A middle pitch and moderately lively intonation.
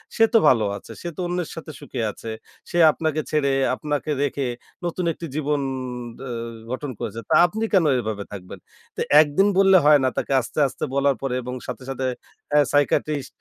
Yes: medium, 145 Hz; average, 3.5 semitones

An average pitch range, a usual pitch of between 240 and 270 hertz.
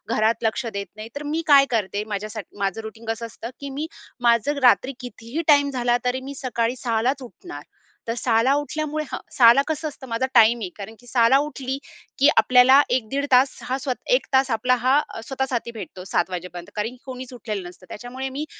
Yes: average, 3.3 semitones; high, 245 Hz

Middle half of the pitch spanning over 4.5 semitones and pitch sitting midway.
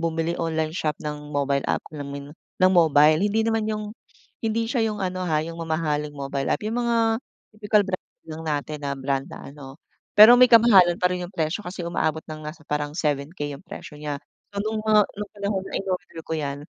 Yes: average, 5.3 semitones; medium, 165 Hz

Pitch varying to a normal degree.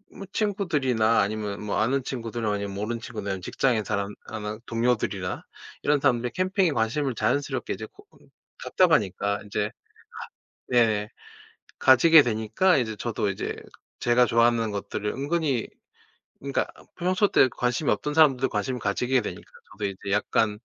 Yes: average, 4.7 semitones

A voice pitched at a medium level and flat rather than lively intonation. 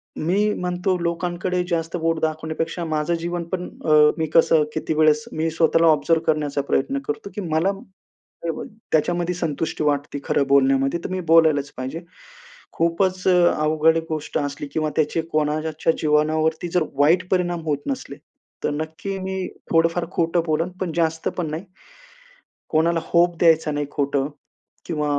Yes: medium, 160 Hz; narrow, 2.2 semitones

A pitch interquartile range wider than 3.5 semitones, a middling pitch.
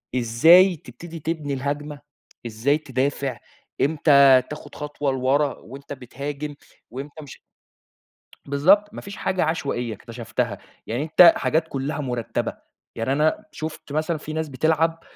No: average, 3.1 semitones; medium, 145 Hz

